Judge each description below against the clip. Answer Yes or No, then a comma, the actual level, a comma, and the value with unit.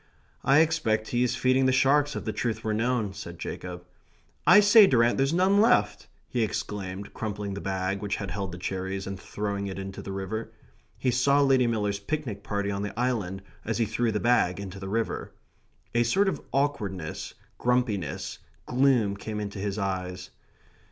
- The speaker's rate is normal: Yes, average, 180 wpm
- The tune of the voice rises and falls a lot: No, average, 4.4 semitones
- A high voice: No, low, 105 Hz